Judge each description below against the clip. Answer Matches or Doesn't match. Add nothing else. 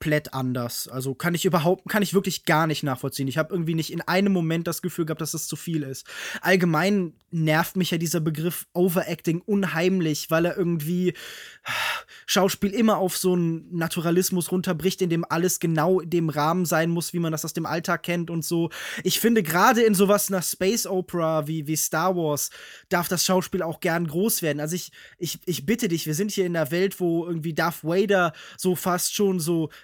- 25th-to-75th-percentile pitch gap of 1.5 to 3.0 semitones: Matches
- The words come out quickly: Matches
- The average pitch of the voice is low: Doesn't match